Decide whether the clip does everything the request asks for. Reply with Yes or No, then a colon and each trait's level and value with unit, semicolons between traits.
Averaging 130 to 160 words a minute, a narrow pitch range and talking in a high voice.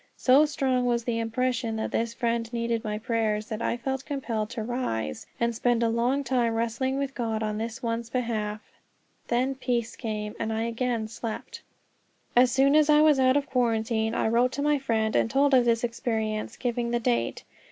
No: average, 195 wpm; narrow, 2.3 semitones; high, 235 Hz